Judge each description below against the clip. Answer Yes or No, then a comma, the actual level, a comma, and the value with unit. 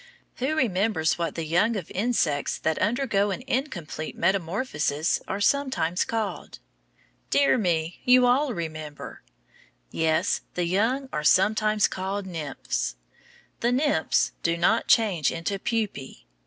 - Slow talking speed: Yes, slow, 125 wpm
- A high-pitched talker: Yes, high, 195 Hz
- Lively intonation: Yes, wide, 6.2 semitones